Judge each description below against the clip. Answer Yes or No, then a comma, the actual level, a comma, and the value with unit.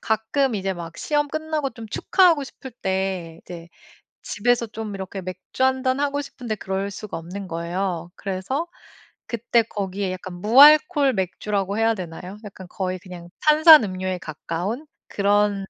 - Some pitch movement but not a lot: No, wide, 5.8 semitones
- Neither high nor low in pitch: No, high, 205 Hz